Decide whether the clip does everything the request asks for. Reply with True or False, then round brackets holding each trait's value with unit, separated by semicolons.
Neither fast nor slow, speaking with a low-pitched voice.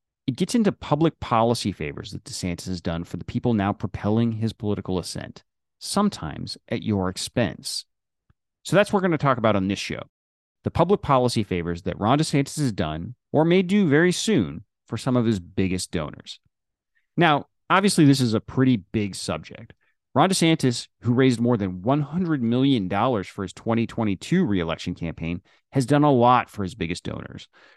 True (175 wpm; 115 Hz)